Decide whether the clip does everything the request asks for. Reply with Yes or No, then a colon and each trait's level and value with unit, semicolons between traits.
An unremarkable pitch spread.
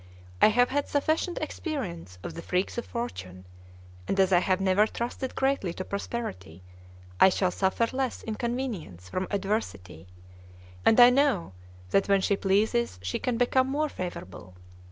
No: wide, 5.9 semitones